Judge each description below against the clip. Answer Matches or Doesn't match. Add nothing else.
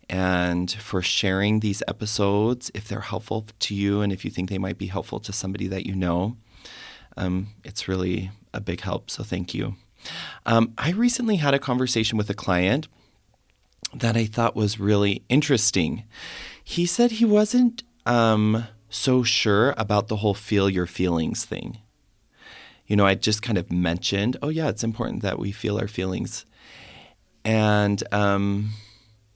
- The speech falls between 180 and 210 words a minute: Doesn't match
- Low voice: Matches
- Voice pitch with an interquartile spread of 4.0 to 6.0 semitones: Doesn't match